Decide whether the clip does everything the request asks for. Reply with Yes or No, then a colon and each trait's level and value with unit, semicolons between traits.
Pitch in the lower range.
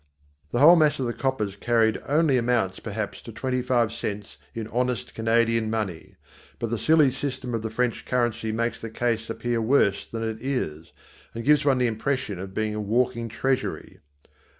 Yes: low, 115 Hz